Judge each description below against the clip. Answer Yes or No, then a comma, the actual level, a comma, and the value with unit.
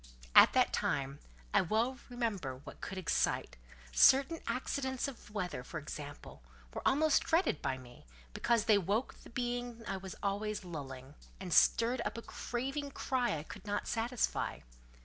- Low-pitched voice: No, high, 210 Hz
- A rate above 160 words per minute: No, average, 155 wpm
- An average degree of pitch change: No, wide, 8.3 semitones